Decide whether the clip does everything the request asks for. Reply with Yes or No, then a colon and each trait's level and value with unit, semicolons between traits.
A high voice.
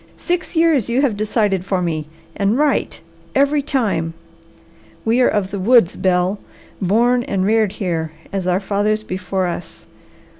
Yes: high, 205 Hz